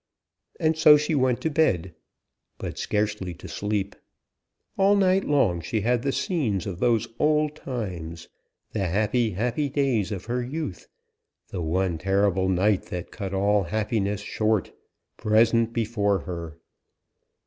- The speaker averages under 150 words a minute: Yes, slow, 135 wpm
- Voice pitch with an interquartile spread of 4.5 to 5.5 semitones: Yes, average, 5.1 semitones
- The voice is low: Yes, low, 105 Hz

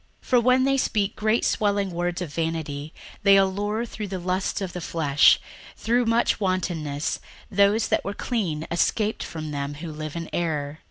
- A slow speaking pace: No, average, 175 wpm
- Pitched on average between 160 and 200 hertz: Yes, medium, 185 Hz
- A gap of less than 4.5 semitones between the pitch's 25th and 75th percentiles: No, average, 4.9 semitones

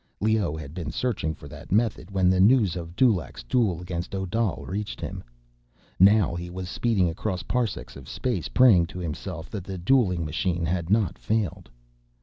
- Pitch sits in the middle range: No, very low, 95 Hz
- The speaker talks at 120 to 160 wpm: No, average, 170 wpm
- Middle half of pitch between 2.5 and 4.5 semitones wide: Yes, average, 4.1 semitones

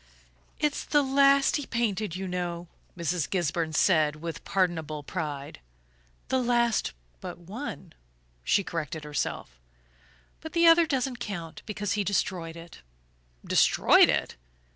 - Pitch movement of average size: No, wide, 6.7 semitones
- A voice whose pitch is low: No, medium, 185 Hz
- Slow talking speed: Yes, slow, 125 wpm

